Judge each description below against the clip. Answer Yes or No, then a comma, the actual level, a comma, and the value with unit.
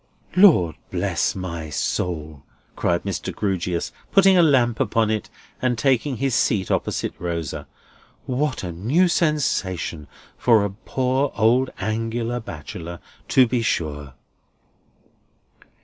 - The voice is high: No, low, 110 Hz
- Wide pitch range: Yes, wide, 6.9 semitones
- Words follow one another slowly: Yes, slow, 115 wpm